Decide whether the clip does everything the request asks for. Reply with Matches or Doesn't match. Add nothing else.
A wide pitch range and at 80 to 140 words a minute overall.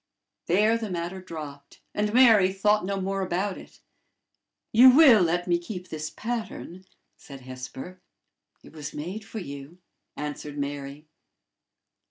Matches